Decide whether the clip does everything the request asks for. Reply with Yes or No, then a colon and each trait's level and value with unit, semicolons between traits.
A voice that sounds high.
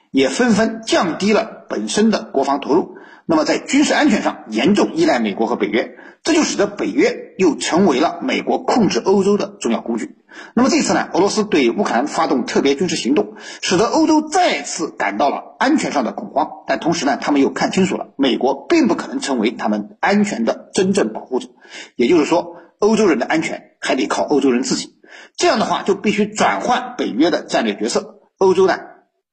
Yes: high, 240 Hz